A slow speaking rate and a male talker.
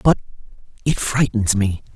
Yes: slow, 125 wpm; male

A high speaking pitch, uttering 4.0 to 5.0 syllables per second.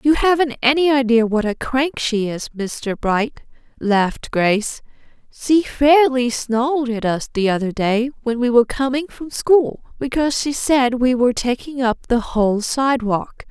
Yes: very high, 250 Hz; 4.5 syllables/s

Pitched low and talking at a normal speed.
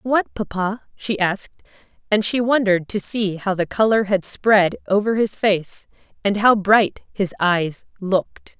No: high, 200 Hz; average, 160 wpm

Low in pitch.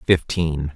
Yes: very low, 80 Hz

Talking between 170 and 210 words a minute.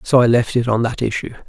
No: fast, 285 wpm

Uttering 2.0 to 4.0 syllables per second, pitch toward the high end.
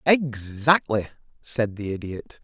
No: 3.6 syllables/s; low, 120 Hz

